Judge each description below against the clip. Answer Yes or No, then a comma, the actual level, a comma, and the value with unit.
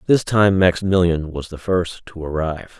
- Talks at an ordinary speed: Yes, average, 170 wpm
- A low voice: Yes, very low, 90 Hz